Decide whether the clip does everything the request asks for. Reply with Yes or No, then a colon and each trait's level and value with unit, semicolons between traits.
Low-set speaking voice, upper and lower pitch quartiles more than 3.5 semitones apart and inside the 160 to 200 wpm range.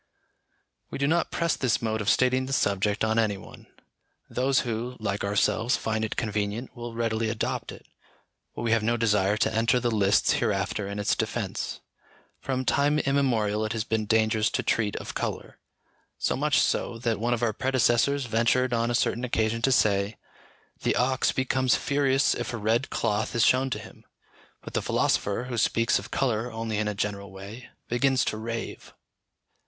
No: low, 115 Hz; average, 2.8 semitones; average, 180 wpm